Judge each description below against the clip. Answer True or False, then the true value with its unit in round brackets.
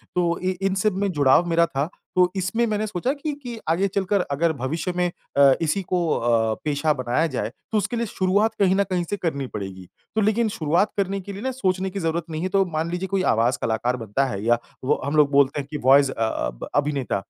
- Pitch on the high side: False (170 Hz)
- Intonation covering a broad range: True (6.0 semitones)